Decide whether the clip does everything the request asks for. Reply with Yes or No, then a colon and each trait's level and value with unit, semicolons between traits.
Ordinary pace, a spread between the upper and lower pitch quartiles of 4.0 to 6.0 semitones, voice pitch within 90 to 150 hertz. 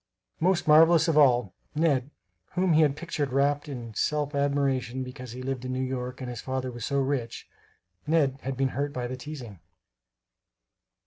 No: average, 175 wpm; narrow, 2.6 semitones; low, 135 Hz